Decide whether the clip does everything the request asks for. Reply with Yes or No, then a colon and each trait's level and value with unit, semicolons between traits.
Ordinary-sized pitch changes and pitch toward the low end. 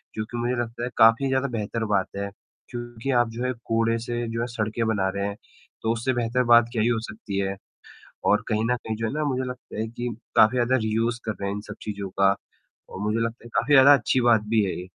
No: narrow, 2.0 semitones; low, 115 Hz